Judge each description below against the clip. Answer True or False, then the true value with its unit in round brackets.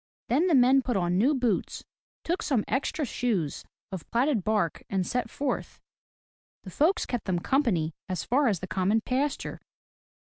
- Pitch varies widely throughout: True (6.4 semitones)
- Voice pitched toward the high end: True (235 Hz)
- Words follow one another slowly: False (165 wpm)